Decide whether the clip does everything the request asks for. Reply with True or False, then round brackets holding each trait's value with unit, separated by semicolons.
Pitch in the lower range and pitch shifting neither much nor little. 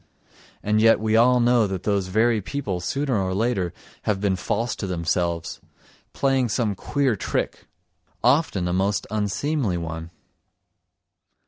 True (105 Hz; 4.6 semitones)